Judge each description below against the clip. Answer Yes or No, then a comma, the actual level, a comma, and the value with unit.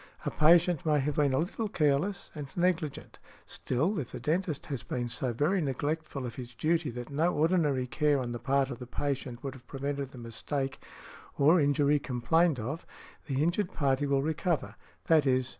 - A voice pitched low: No, medium, 145 Hz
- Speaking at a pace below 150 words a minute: No, average, 180 wpm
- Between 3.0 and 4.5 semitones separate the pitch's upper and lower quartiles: Yes, average, 3.4 semitones